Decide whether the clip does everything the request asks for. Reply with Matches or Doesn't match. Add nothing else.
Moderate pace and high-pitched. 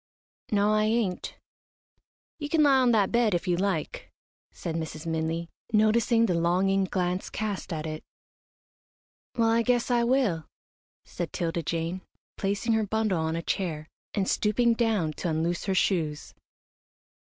Matches